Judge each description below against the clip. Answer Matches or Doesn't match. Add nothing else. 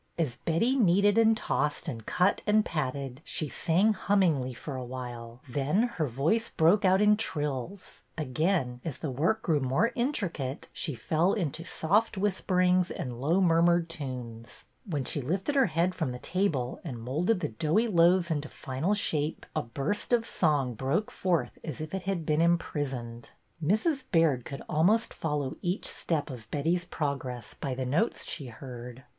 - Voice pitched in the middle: Matches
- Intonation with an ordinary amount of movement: Doesn't match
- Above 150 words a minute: Matches